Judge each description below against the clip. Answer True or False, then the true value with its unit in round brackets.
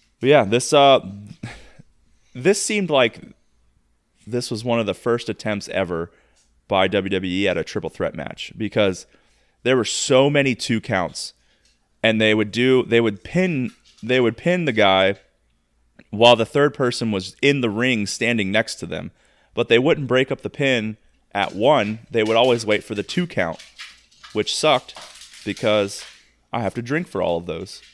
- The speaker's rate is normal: True (175 wpm)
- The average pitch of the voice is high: False (115 Hz)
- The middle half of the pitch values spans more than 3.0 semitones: True (4.3 semitones)